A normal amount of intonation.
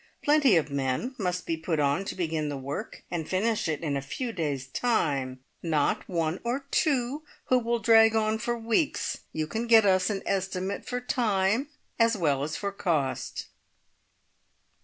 No: wide, 6.9 semitones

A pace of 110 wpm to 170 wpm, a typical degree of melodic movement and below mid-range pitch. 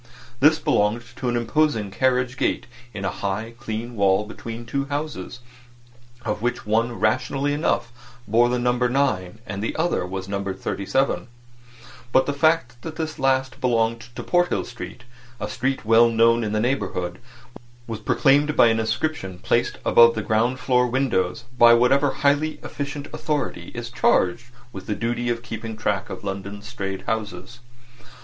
Yes: average, 160 wpm; average, 3.6 semitones; low, 120 Hz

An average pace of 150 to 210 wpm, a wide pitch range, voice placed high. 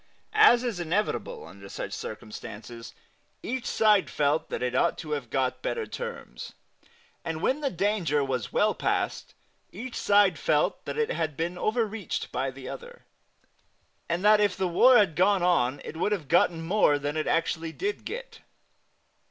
No: average, 170 wpm; wide, 6.7 semitones; medium, 175 Hz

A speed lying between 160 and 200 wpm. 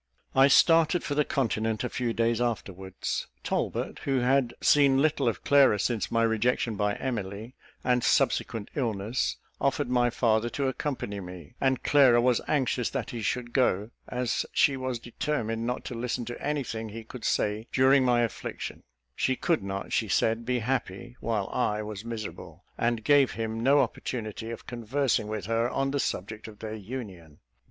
Yes: average, 175 wpm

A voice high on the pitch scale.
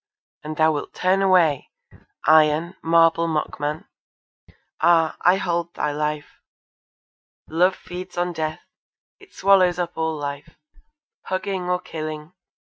No: medium, 165 Hz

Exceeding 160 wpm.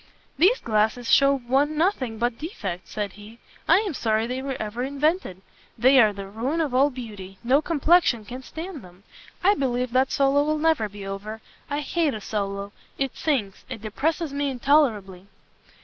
Yes: average, 175 wpm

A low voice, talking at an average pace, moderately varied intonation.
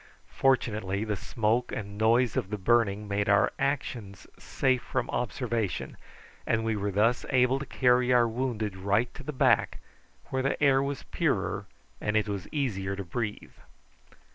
Yes: low, 115 Hz; average, 160 wpm; average, 3.7 semitones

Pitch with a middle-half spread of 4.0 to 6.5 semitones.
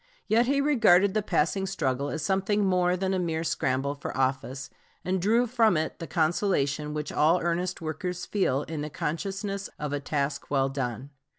Yes: average, 5.2 semitones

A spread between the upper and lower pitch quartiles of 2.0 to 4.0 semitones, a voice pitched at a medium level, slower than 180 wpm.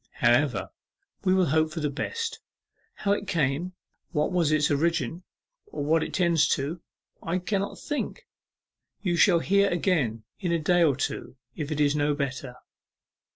Yes: average, 3.7 semitones; medium, 165 Hz; average, 160 wpm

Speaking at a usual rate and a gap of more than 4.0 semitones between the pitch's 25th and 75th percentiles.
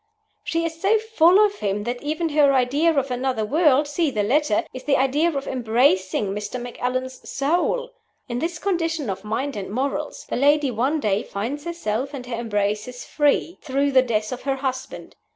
Yes: average, 185 wpm; average, 4.5 semitones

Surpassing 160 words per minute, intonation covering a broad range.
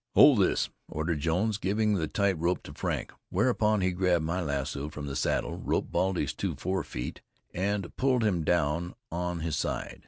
No: average, 175 wpm; average, 3.9 semitones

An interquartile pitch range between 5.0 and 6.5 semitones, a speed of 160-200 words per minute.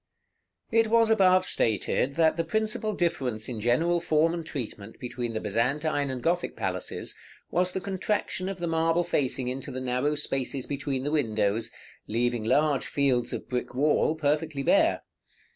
Yes: wide, 5.6 semitones; average, 165 wpm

